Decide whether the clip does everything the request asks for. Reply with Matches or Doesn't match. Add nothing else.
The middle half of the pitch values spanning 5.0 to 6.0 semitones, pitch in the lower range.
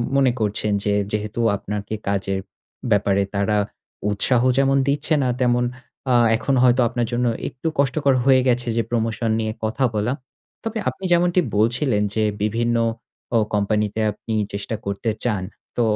Doesn't match